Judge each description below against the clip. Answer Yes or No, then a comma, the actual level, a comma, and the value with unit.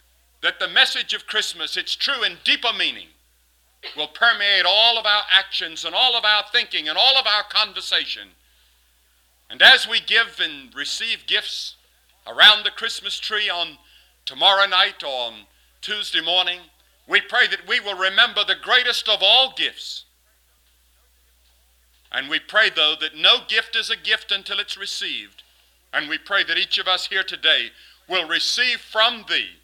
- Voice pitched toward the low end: No, high, 190 Hz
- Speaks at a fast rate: No, average, 165 wpm